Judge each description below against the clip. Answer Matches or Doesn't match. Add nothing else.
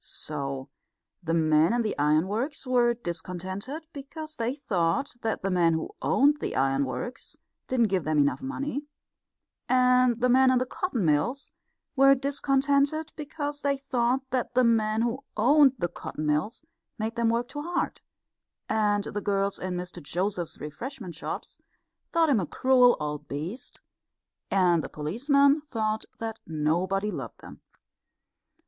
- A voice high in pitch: Matches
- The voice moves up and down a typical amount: Doesn't match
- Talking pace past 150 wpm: Doesn't match